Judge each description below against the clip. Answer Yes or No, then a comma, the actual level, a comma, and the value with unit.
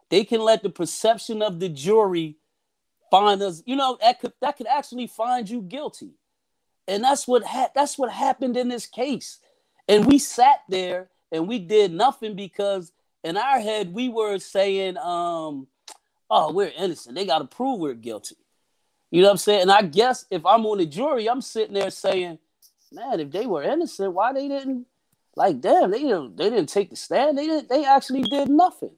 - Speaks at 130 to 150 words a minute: No, average, 195 wpm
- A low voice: No, high, 230 Hz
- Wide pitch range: Yes, wide, 5.7 semitones